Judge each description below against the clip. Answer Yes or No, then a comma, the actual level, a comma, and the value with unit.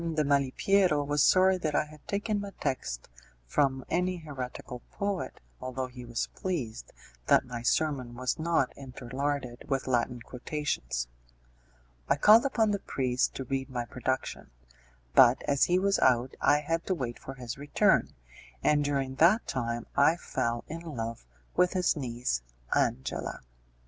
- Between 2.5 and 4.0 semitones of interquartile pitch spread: No, average, 4.9 semitones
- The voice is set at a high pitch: No, low, 135 Hz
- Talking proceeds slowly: No, average, 150 wpm